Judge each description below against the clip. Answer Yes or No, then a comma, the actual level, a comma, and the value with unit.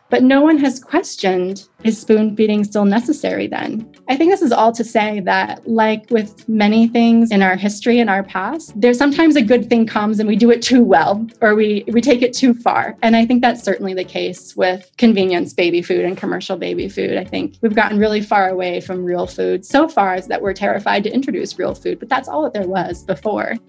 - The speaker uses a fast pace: Yes, fast, 230 wpm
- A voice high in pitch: Yes, high, 215 Hz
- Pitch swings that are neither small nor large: Yes, average, 4.1 semitones